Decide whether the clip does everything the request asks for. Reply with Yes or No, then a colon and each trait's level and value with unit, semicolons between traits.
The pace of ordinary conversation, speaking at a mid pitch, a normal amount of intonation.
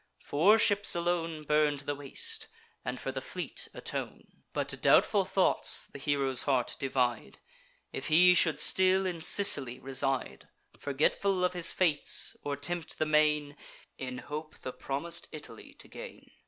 Yes: average, 150 wpm; medium, 150 Hz; average, 4.6 semitones